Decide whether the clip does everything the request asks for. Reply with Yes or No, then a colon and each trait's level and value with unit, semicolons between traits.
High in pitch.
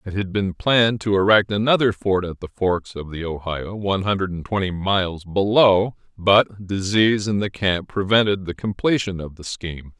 No: very low, 95 Hz